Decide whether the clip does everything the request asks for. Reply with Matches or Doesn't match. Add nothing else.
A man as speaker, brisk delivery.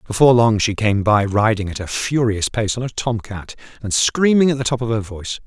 Matches